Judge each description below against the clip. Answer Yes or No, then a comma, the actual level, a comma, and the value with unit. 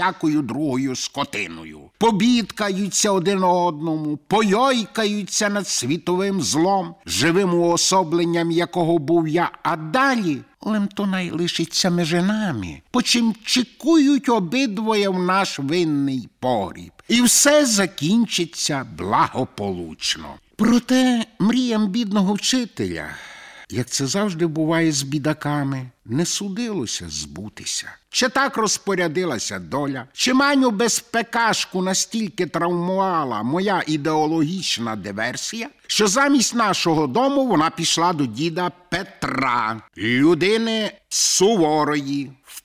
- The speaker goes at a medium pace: No, slow, 100 wpm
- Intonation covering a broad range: Yes, wide, 6.1 semitones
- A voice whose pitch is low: No, medium, 180 Hz